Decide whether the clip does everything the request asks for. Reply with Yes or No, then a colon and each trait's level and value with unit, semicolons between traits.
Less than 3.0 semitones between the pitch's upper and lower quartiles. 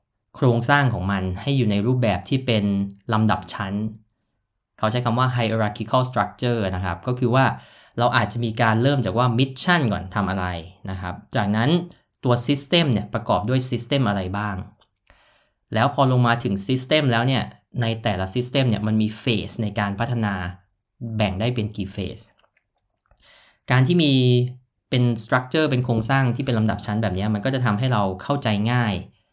No: average, 3.5 semitones